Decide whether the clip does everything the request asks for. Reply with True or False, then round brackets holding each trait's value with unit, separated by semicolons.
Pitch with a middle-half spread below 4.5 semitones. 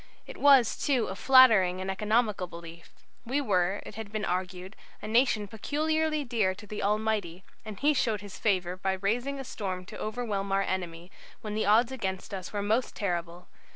True (3.9 semitones)